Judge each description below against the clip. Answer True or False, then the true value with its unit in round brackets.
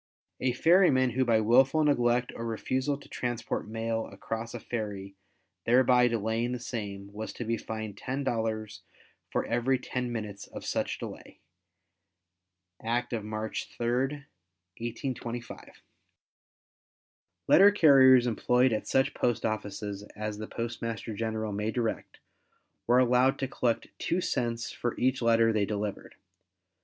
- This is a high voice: False (115 Hz)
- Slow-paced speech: True (130 wpm)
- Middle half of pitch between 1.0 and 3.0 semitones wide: True (2.5 semitones)